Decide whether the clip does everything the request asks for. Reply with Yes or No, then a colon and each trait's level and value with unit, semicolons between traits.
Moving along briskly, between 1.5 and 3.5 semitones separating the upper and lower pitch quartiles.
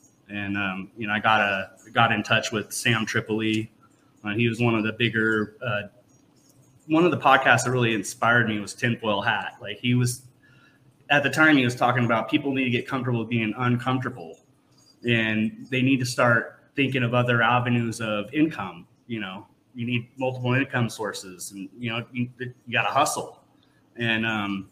No: average, 190 wpm; average, 2.8 semitones